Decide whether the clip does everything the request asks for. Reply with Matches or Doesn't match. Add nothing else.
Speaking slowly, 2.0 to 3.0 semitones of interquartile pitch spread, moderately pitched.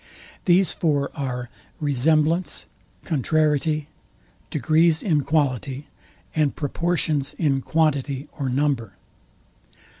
Matches